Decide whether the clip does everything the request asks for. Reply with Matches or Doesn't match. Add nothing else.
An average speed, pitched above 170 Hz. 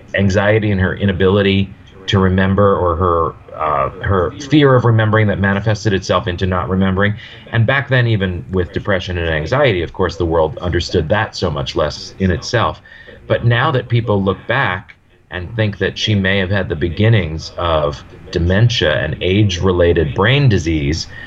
Doesn't match